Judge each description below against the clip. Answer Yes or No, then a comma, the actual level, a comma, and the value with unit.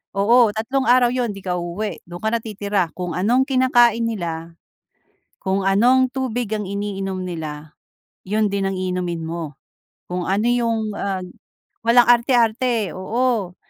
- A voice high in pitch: Yes, high, 205 Hz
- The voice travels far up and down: No, average, 4.6 semitones